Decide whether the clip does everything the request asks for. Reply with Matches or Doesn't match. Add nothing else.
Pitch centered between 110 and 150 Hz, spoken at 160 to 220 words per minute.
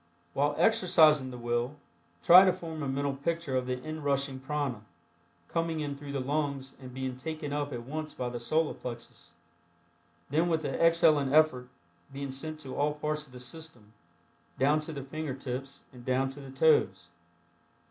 Matches